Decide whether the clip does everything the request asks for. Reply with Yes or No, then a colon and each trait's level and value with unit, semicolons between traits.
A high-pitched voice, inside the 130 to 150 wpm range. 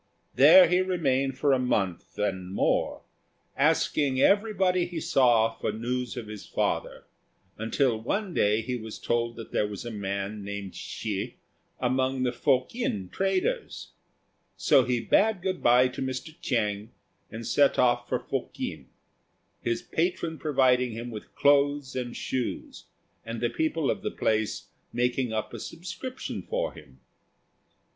No: low, 125 Hz; average, 145 wpm